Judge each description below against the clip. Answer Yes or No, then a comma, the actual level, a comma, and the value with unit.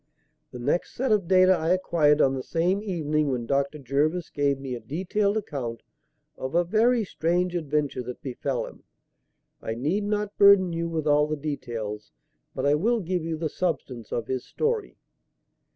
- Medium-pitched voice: Yes, medium, 155 Hz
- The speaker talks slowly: No, average, 175 wpm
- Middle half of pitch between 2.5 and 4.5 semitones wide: No, average, 5.2 semitones